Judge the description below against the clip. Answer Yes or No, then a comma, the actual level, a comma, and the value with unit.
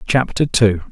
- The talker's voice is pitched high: No, low, 115 Hz